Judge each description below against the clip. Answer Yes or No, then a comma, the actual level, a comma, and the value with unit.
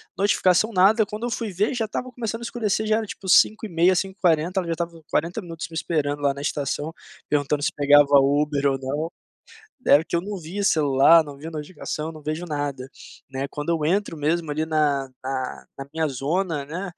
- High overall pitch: No, medium, 160 Hz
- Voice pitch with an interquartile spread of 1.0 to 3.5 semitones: No, average, 4.7 semitones